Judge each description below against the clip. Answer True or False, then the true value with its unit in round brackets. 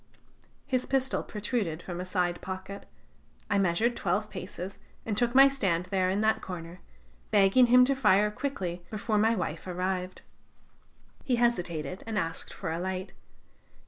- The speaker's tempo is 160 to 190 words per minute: False (150 wpm)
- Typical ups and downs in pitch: True (4.2 semitones)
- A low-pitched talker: False (195 Hz)